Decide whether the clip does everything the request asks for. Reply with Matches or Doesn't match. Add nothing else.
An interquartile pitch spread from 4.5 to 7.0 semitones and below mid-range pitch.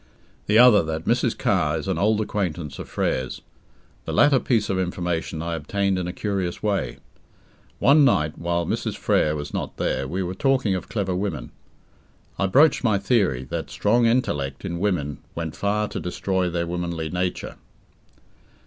Doesn't match